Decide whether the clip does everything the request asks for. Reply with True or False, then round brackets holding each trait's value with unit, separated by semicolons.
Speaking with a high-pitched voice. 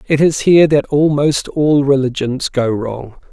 False (140 Hz)